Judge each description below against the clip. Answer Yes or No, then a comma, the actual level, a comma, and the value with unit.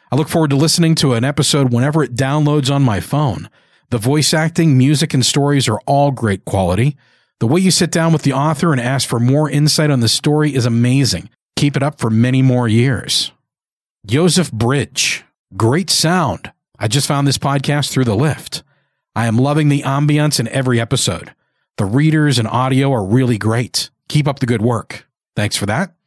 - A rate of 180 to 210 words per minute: Yes, average, 195 wpm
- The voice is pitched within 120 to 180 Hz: Yes, medium, 140 Hz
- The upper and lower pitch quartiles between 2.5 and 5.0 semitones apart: Yes, average, 3.8 semitones